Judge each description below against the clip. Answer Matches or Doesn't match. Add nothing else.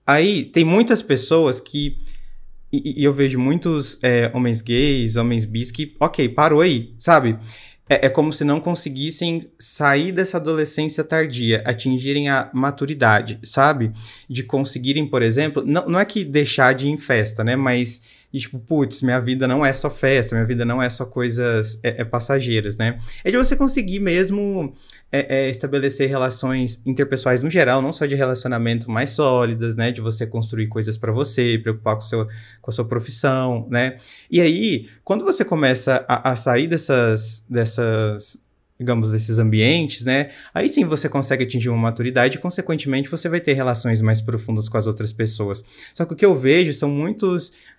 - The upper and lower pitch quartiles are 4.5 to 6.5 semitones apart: Doesn't match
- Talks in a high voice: Doesn't match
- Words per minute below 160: Doesn't match